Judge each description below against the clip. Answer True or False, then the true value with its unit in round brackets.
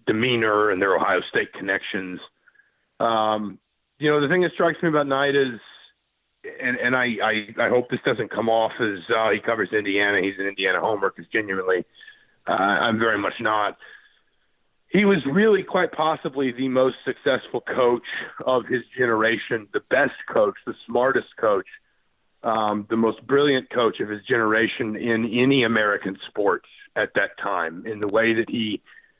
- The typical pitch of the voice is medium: False (130 Hz)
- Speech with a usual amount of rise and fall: False (7.2 semitones)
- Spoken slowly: False (165 wpm)